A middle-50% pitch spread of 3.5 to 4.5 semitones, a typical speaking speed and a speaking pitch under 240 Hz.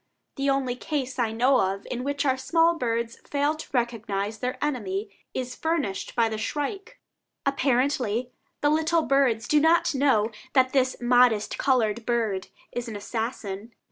No: average, 3.8 semitones; average, 155 wpm; very high, 250 Hz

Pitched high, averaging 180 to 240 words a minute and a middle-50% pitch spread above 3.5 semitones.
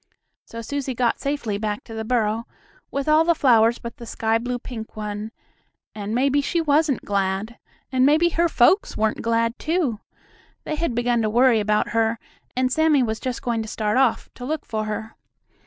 Yes: high, 235 Hz; average, 190 wpm; average, 4.1 semitones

